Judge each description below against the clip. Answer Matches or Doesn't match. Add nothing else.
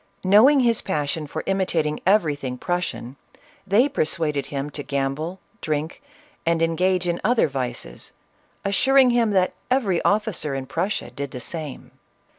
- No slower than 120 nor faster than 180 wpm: Matches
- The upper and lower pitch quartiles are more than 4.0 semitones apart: Matches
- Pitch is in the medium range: Matches